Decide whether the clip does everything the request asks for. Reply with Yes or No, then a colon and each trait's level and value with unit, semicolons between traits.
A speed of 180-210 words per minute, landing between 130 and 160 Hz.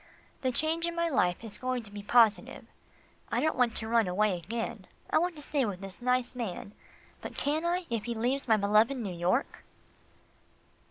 No: average, 195 wpm; high, 235 Hz